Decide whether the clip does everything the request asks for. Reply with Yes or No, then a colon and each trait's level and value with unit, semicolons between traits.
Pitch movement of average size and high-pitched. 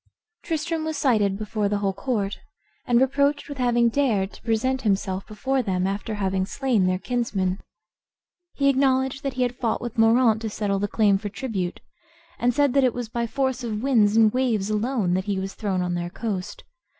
Yes: average, 4.6 semitones; high, 225 Hz